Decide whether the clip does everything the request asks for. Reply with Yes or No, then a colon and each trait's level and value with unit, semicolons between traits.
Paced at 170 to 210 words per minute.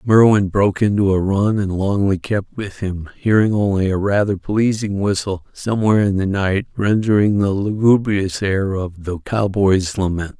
No: average, 160 wpm